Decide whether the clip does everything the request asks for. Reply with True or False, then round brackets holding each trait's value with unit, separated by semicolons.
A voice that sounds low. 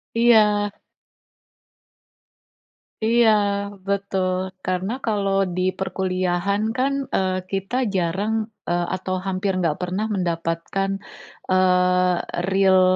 False (190 Hz)